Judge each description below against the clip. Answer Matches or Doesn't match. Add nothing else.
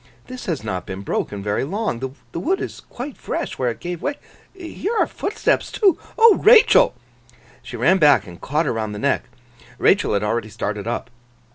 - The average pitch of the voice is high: Doesn't match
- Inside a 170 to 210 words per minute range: Matches